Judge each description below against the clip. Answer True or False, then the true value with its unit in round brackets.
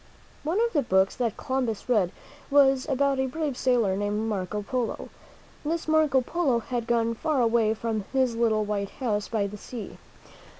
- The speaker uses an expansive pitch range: False (4.1 semitones)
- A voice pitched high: True (235 Hz)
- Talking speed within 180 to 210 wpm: False (170 wpm)